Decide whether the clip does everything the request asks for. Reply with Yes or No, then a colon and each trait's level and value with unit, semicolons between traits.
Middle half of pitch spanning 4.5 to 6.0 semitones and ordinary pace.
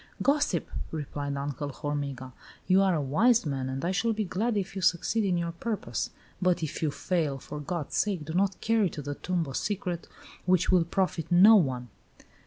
Yes: average, 5.1 semitones; average, 195 wpm